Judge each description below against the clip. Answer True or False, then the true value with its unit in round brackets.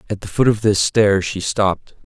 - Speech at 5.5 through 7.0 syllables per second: False (5.0 syllables/s)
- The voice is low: True (100 Hz)